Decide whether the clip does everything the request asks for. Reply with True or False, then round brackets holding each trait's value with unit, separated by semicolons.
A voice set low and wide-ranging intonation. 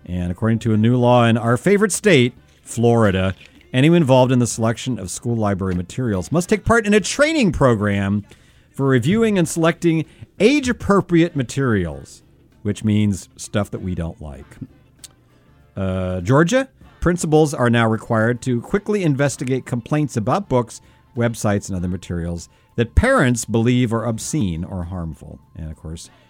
True (120 Hz; 7.1 semitones)